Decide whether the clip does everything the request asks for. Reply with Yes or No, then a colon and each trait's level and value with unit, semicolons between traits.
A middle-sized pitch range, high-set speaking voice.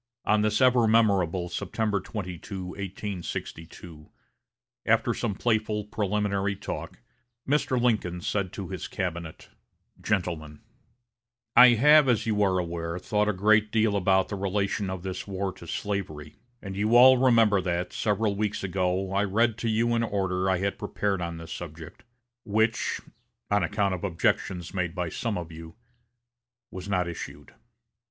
No: average, 3.0 semitones; low, 100 Hz